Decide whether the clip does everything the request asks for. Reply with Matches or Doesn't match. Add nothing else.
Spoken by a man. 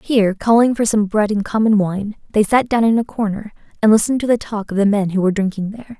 Doesn't match